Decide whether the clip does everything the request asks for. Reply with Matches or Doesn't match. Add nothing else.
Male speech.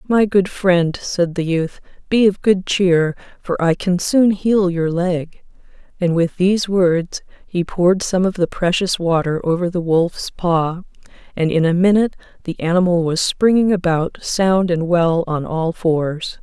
Doesn't match